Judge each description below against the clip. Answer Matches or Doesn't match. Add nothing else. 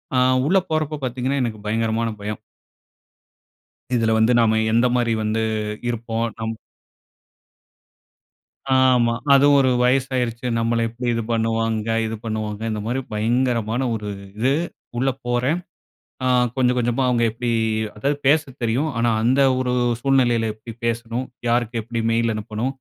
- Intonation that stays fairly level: Matches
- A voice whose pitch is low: Matches